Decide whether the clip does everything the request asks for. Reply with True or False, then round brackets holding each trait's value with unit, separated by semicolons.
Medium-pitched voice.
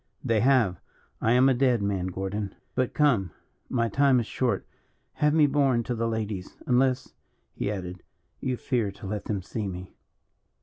False (115 Hz)